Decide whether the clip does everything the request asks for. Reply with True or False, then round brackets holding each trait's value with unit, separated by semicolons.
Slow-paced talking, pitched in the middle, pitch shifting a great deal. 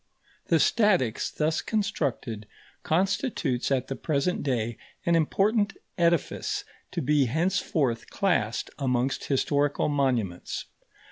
True (105 wpm; 145 Hz; 5.9 semitones)